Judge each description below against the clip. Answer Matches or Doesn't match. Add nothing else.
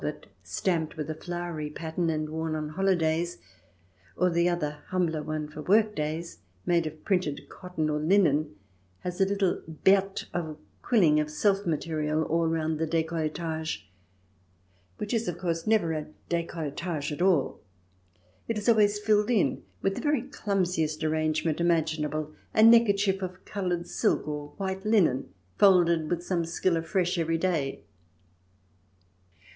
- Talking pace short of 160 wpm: Matches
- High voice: Doesn't match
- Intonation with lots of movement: Doesn't match